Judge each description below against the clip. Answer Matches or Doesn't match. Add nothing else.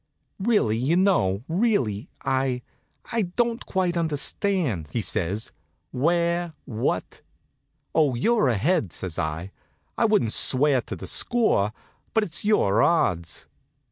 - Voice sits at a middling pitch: Matches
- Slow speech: Matches